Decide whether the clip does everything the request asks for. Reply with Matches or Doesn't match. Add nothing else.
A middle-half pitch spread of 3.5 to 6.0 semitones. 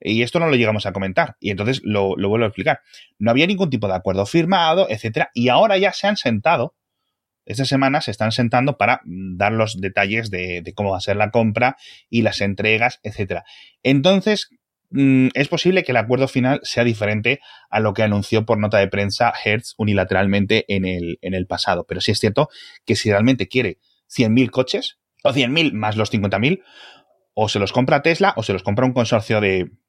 Matches